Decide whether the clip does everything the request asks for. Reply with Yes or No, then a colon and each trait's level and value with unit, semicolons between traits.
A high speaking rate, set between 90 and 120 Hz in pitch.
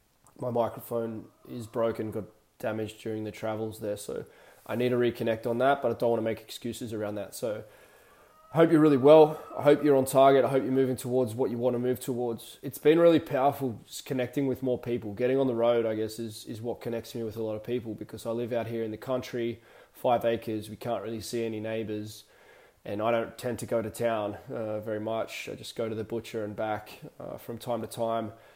Yes: fast, 235 wpm; low, 115 Hz